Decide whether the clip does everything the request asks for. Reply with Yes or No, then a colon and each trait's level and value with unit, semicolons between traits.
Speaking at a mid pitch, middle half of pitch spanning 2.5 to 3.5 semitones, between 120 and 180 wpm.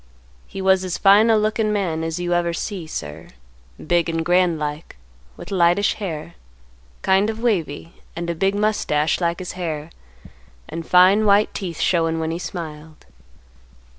Yes: medium, 175 Hz; average, 3.2 semitones; average, 160 wpm